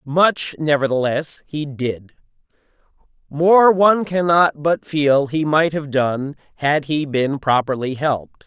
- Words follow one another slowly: Yes, slow, 130 wpm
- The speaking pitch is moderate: Yes, medium, 150 Hz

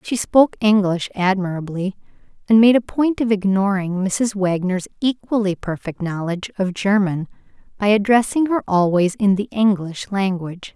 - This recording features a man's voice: No, female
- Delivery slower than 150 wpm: Yes, average, 140 wpm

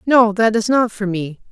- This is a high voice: Yes, high, 215 Hz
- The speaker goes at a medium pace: No, fast, 235 wpm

